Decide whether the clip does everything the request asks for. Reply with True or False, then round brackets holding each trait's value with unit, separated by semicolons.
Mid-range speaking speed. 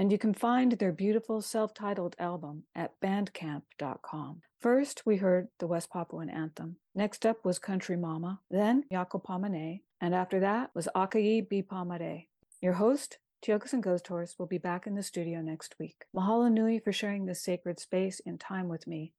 True (180 wpm)